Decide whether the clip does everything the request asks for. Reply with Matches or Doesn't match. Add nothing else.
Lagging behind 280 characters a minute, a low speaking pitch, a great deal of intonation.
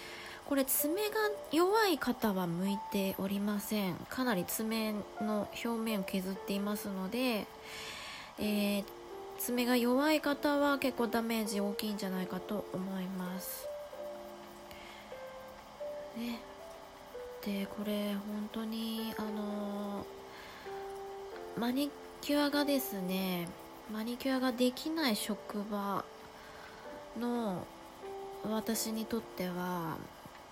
Doesn't match